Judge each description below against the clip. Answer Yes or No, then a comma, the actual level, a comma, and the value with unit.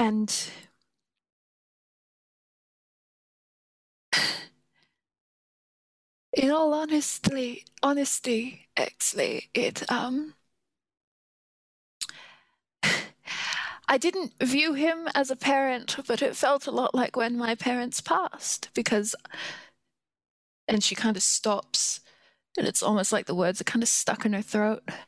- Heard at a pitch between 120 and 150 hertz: No, very high, 250 Hz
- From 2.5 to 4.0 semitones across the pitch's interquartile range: No, average, 5.0 semitones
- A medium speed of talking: No, slow, 105 wpm